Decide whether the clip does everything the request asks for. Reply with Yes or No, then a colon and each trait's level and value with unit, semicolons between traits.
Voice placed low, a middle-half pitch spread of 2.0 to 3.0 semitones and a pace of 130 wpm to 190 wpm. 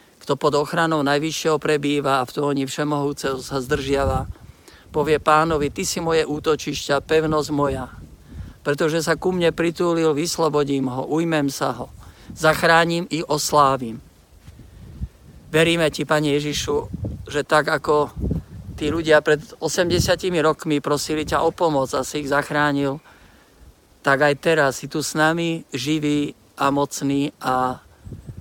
No: medium, 145 Hz; narrow, 2.6 semitones; average, 135 wpm